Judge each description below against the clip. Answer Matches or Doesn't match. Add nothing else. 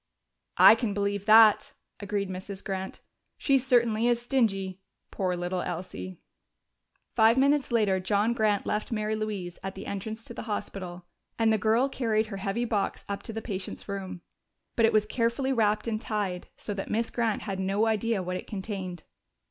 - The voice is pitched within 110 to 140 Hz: Doesn't match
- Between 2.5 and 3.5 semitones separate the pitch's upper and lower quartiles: Matches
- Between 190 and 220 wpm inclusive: Doesn't match